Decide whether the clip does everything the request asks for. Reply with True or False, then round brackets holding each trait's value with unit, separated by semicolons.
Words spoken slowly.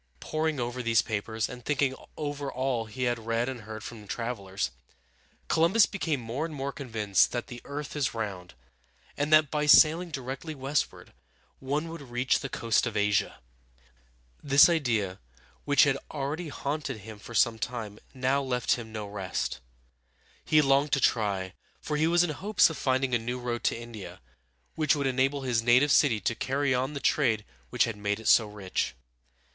False (175 wpm)